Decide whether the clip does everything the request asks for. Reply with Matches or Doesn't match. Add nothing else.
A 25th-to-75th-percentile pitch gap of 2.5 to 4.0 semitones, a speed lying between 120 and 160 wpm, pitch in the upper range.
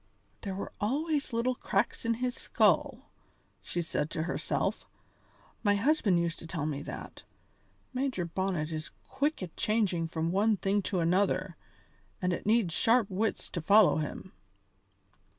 Doesn't match